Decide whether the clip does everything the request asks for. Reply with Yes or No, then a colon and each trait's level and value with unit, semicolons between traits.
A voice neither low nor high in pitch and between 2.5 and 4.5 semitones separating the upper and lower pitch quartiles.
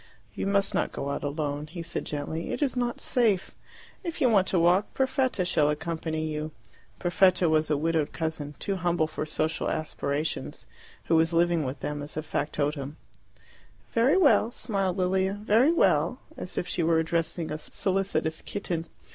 Yes: medium, 170 Hz; average, 4.0 semitones